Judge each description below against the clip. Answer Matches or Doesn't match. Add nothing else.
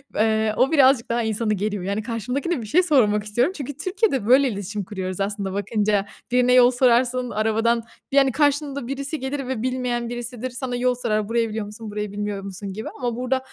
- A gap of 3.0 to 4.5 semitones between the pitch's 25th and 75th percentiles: Matches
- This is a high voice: Matches